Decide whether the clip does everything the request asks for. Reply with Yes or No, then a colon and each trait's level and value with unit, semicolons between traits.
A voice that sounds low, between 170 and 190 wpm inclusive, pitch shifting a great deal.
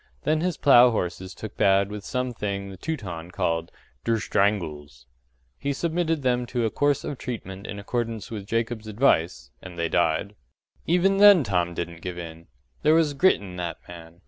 Yes: low, 105 Hz; average, 175 wpm; wide, 6.6 semitones